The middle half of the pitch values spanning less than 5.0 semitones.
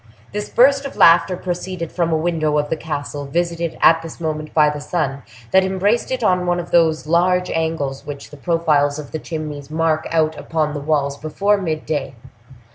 Yes: average, 2.7 semitones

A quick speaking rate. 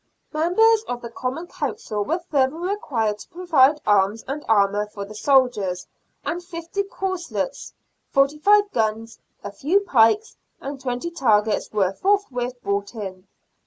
No: average, 140 wpm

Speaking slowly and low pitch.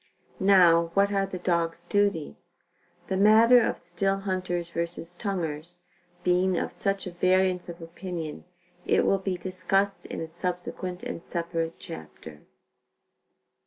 No: slow, 125 wpm; medium, 180 Hz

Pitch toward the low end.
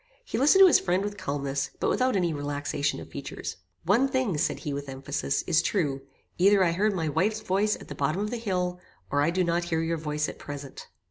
No: medium, 175 Hz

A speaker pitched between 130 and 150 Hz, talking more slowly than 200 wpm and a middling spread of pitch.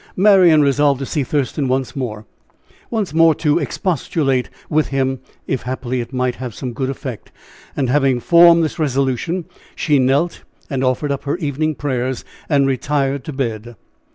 Yes: low, 135 Hz; average, 160 wpm; average, 3.1 semitones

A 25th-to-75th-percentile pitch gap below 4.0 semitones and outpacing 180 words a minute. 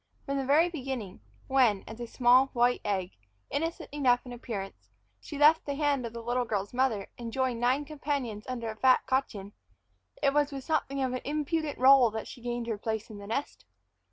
Yes: average, 3.6 semitones; average, 200 wpm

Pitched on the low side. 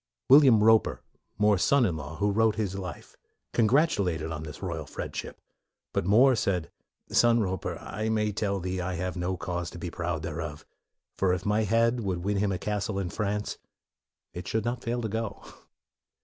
Yes: low, 100 Hz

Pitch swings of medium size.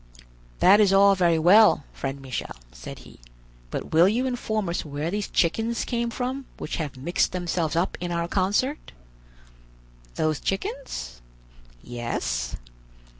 No: wide, 6.1 semitones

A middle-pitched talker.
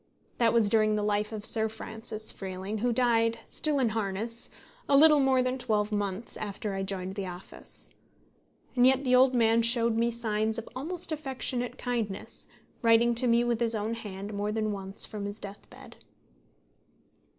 No: high, 225 Hz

